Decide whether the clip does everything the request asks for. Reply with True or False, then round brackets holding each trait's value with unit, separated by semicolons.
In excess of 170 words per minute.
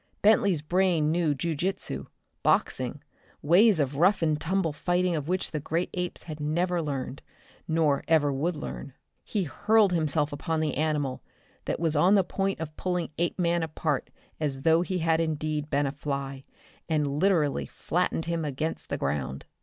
False (165 wpm)